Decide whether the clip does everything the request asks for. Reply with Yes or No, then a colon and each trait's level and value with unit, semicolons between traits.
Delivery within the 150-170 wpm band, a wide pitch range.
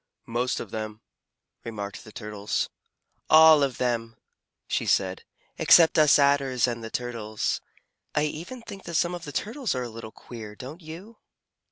Yes: average, 160 wpm; wide, 6.0 semitones